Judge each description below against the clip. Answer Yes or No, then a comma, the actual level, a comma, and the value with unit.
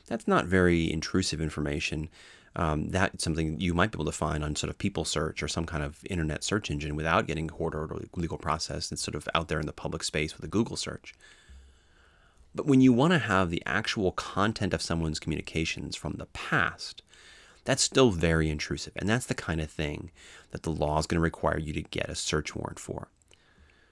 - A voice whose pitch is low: Yes, very low, 80 Hz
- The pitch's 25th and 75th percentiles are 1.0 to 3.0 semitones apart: Yes, average, 2.7 semitones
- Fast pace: Yes, fast, 215 wpm